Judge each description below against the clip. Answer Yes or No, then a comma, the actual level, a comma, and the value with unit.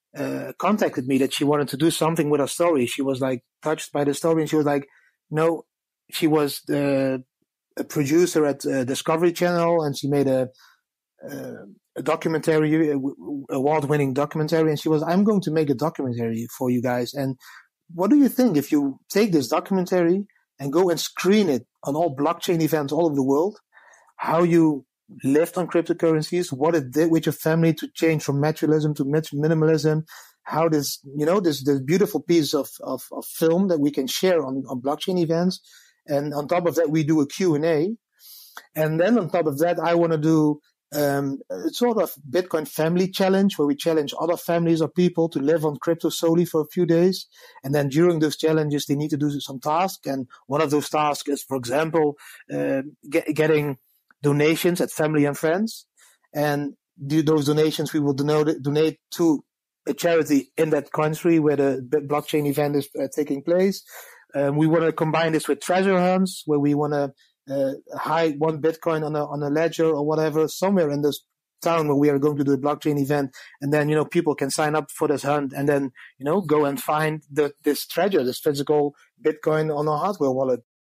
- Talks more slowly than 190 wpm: No, fast, 205 wpm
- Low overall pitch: No, medium, 155 Hz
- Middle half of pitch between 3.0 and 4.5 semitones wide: No, narrow, 2.6 semitones